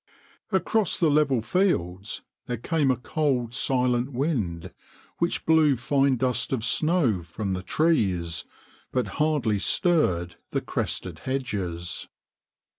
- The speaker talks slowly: Yes, slow, 115 wpm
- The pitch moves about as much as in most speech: No, wide, 7.7 semitones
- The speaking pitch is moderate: No, low, 125 Hz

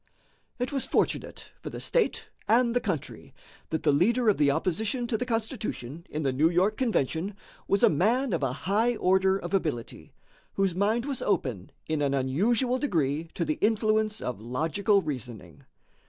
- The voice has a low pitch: No, high, 190 Hz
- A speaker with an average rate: Yes, average, 170 wpm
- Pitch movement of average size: No, wide, 7.2 semitones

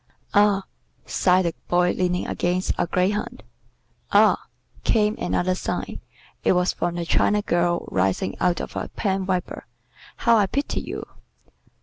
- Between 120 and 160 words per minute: Yes, average, 140 wpm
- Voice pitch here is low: No, medium, 180 Hz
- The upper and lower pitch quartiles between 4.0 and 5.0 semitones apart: No, narrow, 2.5 semitones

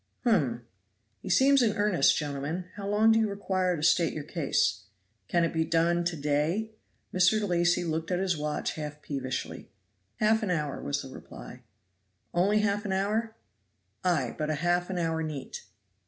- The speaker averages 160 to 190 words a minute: Yes, average, 170 wpm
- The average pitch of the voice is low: No, medium, 175 Hz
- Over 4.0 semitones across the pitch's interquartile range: Yes, average, 4.9 semitones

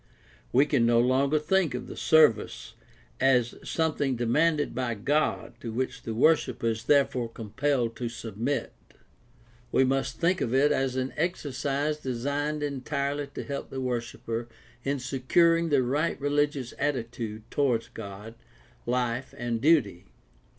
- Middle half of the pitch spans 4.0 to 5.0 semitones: No, average, 3.6 semitones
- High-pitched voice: No, low, 130 Hz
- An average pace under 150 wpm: Yes, average, 140 wpm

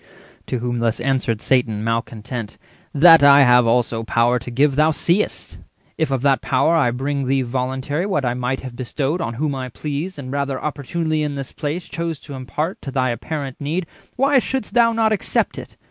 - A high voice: No, low, 135 Hz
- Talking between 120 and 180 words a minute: No, average, 195 wpm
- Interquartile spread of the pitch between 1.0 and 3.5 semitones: No, average, 4.0 semitones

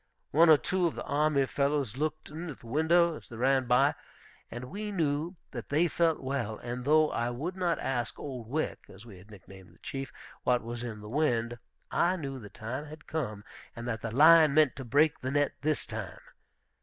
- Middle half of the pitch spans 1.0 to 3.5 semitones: No, average, 4.6 semitones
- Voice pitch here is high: No, medium, 140 Hz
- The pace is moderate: No, fast, 210 wpm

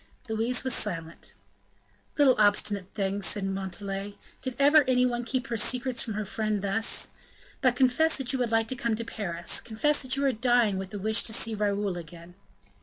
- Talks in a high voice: Yes, high, 220 Hz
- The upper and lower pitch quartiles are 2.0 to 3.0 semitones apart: No, average, 4.0 semitones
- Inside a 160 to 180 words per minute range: No, average, 190 wpm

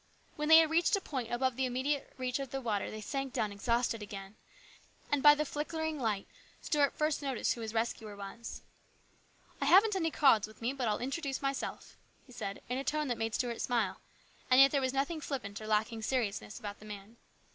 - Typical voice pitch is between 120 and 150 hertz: No, very high, 255 Hz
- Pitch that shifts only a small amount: No, average, 4.6 semitones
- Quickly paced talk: Yes, fast, 215 wpm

